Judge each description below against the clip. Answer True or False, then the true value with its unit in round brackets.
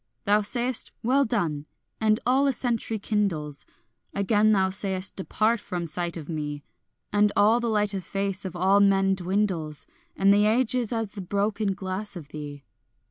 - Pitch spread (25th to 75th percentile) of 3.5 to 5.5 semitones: False (3.0 semitones)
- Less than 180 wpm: True (170 wpm)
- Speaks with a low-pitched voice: False (200 Hz)